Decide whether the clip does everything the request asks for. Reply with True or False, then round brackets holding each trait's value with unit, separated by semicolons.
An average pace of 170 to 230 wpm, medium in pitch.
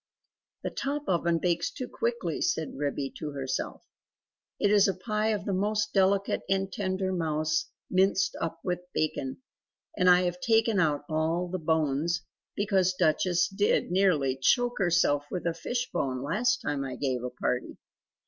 False (160 wpm; 180 Hz)